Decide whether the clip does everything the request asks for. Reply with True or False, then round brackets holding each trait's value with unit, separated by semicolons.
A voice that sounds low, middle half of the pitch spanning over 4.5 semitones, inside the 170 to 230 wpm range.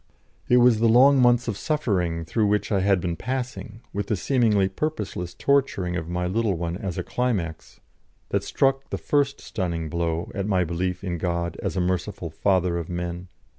True (95 Hz; 5.5 semitones; 185 wpm)